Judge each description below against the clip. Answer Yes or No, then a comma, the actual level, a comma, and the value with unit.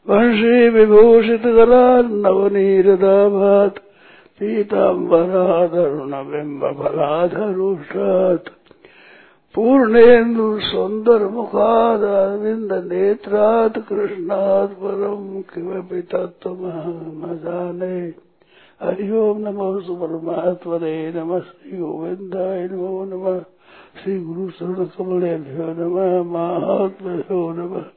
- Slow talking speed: Yes, slow, 30 wpm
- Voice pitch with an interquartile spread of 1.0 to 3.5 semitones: Yes, average, 2.9 semitones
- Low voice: No, high, 190 Hz